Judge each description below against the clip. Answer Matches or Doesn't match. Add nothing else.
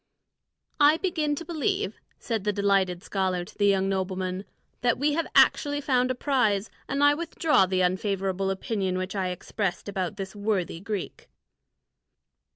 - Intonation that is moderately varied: Doesn't match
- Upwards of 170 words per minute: Doesn't match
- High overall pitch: Matches